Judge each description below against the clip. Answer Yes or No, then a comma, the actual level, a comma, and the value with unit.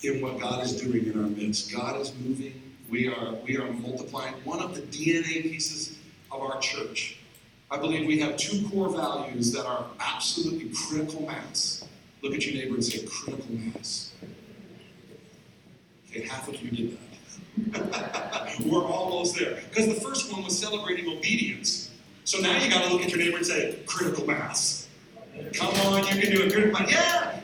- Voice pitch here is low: No, medium, 155 Hz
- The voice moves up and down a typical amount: No, wide, 7.5 semitones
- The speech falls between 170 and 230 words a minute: Yes, average, 175 wpm